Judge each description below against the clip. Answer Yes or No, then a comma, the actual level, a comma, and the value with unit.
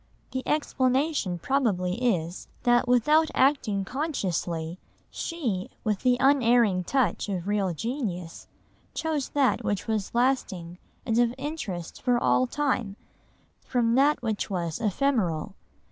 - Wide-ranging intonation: Yes, wide, 6.1 semitones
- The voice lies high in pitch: Yes, high, 235 Hz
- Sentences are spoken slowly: Yes, slow, 120 wpm